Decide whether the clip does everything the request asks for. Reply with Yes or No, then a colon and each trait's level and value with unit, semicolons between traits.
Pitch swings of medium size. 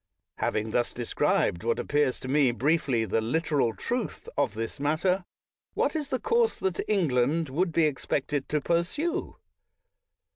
No: wide, 6.0 semitones